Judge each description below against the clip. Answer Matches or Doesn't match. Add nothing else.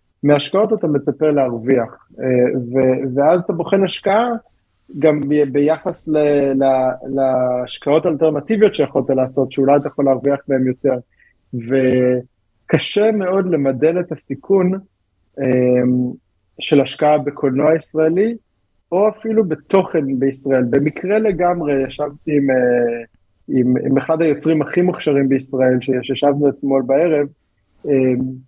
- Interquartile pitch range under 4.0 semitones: Matches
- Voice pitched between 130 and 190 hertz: Matches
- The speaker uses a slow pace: Doesn't match